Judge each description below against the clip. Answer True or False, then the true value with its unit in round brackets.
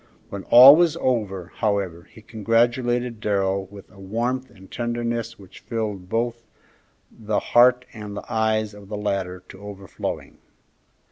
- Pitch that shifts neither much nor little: True (3.2 semitones)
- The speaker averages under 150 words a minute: True (140 wpm)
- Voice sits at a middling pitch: False (110 Hz)